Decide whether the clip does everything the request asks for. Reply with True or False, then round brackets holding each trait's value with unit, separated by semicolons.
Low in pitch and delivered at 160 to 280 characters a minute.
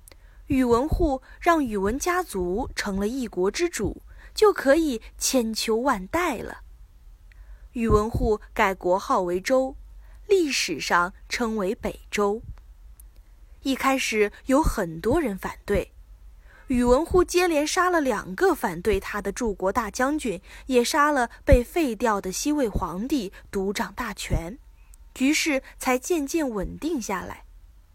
False (245 Hz; 190 characters per minute)